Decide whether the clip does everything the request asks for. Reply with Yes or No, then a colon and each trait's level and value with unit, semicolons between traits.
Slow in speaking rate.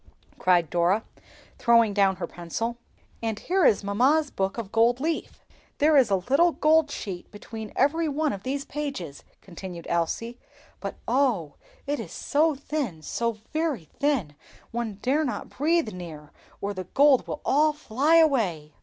No: average, 155 wpm